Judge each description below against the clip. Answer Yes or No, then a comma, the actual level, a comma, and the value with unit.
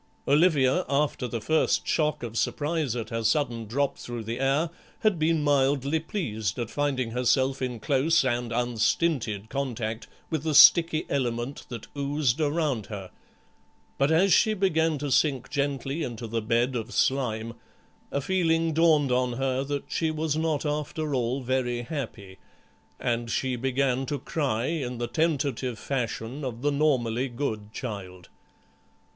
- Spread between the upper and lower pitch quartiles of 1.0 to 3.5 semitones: No, average, 4.2 semitones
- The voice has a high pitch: No, low, 135 Hz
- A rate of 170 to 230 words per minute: No, average, 150 wpm